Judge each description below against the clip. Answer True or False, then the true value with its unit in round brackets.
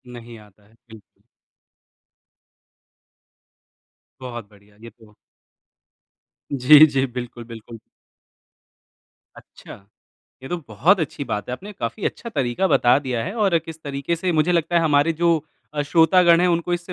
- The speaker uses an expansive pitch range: True (6.3 semitones)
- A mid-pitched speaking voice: True (145 Hz)